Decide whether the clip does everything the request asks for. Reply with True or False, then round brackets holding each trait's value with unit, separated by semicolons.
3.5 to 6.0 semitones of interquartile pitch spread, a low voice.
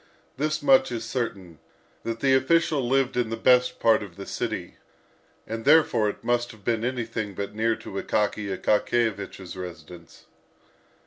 True (3.8 semitones; 115 Hz)